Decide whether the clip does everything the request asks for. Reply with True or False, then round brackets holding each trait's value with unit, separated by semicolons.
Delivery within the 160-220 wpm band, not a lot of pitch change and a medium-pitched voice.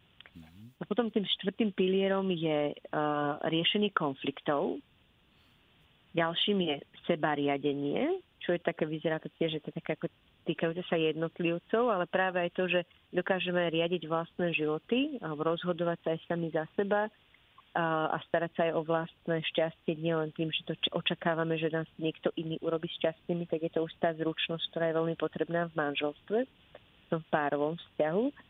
True (165 wpm; 1.8 semitones; 165 Hz)